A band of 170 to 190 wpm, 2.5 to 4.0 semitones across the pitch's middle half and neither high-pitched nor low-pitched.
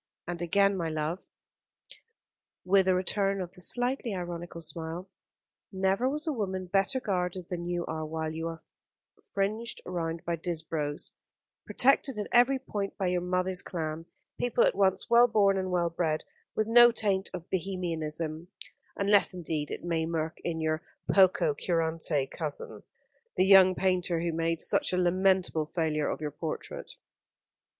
No: average, 155 wpm; average, 3.2 semitones; medium, 180 Hz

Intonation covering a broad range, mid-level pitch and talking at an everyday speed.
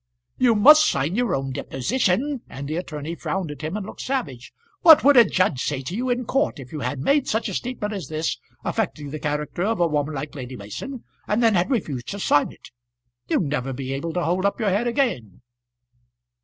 No: wide, 8.5 semitones; medium, 175 Hz; fast, 215 wpm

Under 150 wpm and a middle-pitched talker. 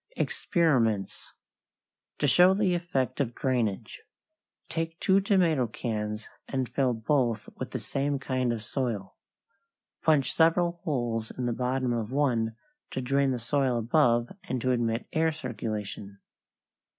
No: slow, 135 wpm; low, 130 Hz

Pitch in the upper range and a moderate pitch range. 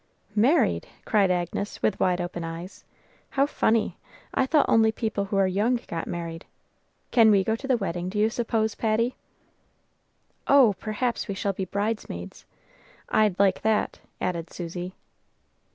Yes: high, 205 Hz; average, 3.7 semitones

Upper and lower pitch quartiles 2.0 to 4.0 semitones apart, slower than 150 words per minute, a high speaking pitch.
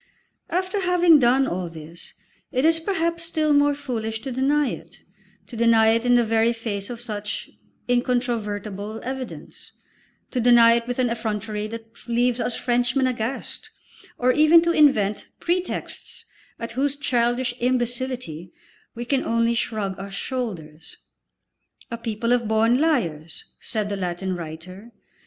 Yes: average, 3.5 semitones; average, 140 wpm; high, 235 Hz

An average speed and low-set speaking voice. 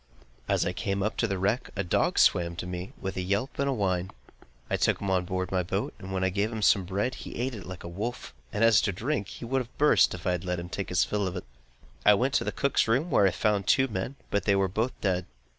No: fast, 275 wpm; low, 100 Hz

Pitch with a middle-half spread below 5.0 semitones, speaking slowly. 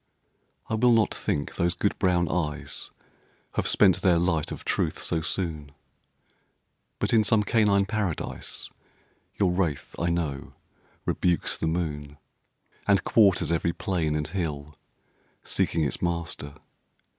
Yes: average, 4.1 semitones; slow, 130 wpm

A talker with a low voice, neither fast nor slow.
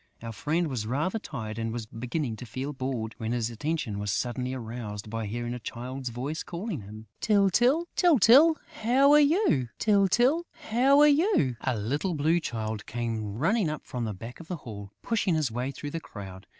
Yes: low, 130 Hz; average, 190 wpm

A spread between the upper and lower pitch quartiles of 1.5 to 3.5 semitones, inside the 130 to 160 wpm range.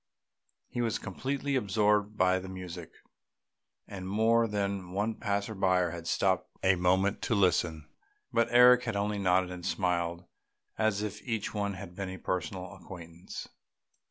Yes: narrow, 2.6 semitones; average, 150 wpm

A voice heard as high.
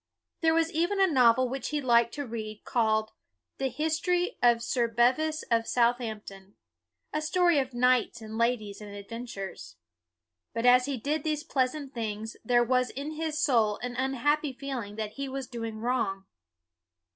Yes: very high, 250 Hz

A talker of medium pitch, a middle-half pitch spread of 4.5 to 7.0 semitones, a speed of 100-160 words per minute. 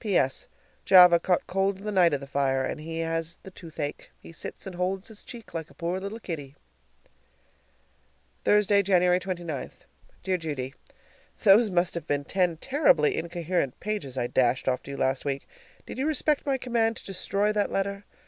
No: medium, 180 Hz; average, 4.8 semitones; average, 175 wpm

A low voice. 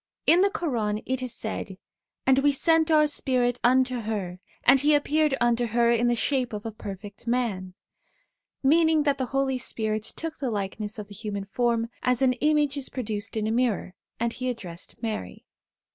No: high, 240 Hz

